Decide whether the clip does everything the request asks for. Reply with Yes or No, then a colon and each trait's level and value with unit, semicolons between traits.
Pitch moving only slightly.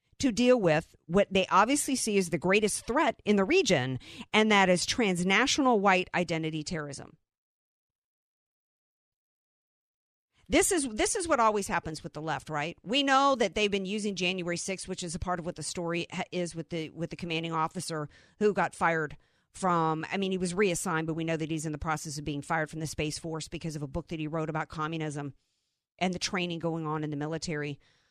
No: average, 3.7 semitones